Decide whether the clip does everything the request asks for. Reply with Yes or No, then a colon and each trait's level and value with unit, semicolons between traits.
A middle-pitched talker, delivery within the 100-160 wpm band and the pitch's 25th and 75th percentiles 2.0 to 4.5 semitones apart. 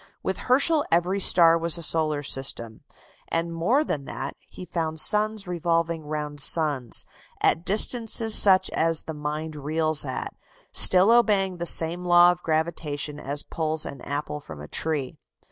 Yes: medium, 165 Hz; average, 155 wpm; average, 3.2 semitones